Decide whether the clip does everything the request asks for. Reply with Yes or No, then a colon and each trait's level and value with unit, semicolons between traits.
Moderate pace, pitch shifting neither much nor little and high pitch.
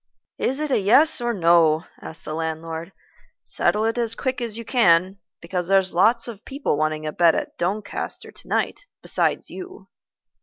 No: average, 165 wpm; wide, 6.2 semitones; high, 195 Hz